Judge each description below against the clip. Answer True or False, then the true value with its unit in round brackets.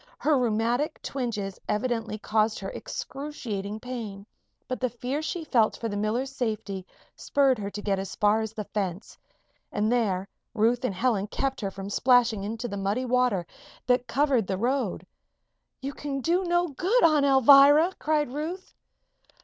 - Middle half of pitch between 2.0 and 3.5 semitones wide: False (4.7 semitones)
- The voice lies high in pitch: True (240 Hz)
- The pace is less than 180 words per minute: True (160 wpm)